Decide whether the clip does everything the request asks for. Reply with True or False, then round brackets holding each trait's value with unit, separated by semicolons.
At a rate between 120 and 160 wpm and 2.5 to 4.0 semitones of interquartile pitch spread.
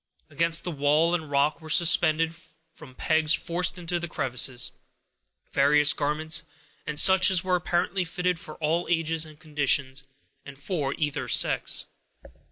True (145 wpm; 2.8 semitones)